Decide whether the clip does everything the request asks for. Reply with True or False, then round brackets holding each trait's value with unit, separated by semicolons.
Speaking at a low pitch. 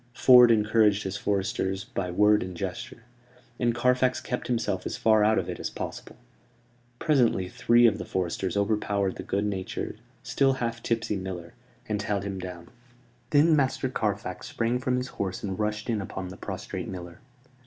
True (105 Hz)